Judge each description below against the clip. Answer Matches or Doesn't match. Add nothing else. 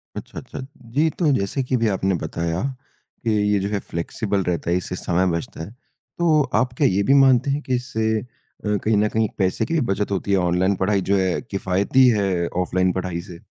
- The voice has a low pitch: Matches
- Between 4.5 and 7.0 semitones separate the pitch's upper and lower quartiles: Matches